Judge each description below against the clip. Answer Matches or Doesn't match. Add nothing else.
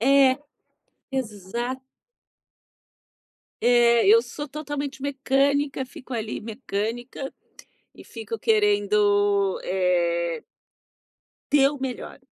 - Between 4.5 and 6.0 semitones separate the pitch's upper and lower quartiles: Matches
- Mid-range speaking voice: Doesn't match